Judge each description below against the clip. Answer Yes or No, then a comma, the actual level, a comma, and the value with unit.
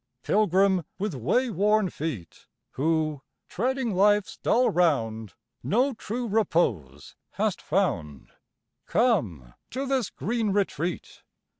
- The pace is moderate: No, slow, 105 wpm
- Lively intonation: Yes, wide, 7.7 semitones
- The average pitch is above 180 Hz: Yes, high, 190 Hz